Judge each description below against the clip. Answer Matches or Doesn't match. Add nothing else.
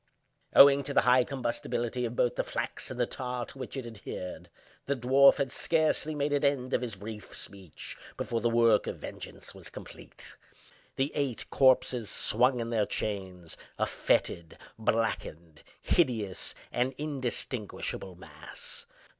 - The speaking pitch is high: Doesn't match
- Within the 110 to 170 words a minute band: Matches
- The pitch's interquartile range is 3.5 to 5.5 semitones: Matches